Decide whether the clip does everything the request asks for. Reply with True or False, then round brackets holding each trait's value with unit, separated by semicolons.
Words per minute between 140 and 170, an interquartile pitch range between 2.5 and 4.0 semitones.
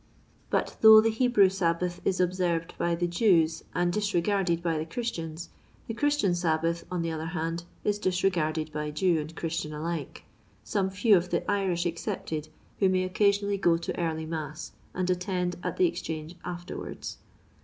True (165 wpm; 2.9 semitones)